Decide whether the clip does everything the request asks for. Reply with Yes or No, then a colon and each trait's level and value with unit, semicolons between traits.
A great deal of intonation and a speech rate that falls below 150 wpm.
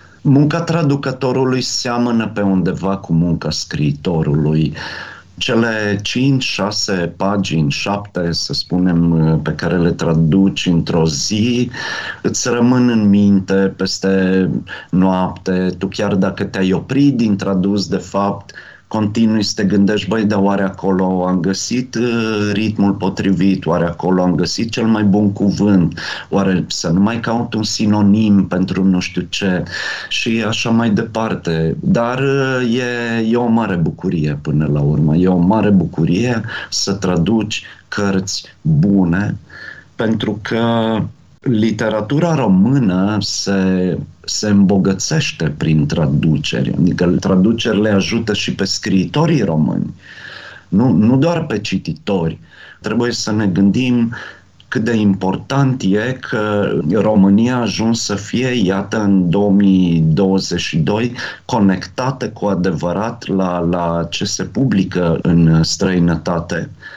No: average, 3.7 semitones; average, 120 wpm